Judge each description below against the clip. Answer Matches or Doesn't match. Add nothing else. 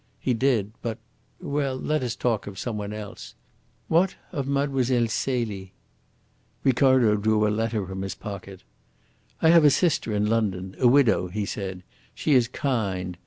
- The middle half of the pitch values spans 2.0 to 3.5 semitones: Doesn't match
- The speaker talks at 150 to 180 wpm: Matches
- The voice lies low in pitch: Matches